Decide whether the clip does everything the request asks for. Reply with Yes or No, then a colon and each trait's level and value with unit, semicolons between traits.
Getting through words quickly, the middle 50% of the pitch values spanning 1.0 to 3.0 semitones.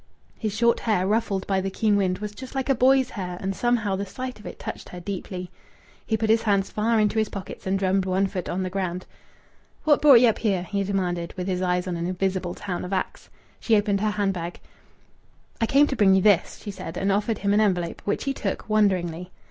Yes: fast, 235 wpm; average, 2.7 semitones